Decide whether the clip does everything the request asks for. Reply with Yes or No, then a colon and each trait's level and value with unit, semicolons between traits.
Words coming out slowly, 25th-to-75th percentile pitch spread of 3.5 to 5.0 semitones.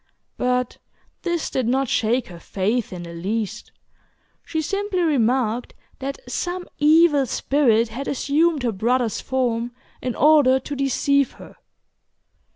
Yes: slow, 130 wpm; average, 4.2 semitones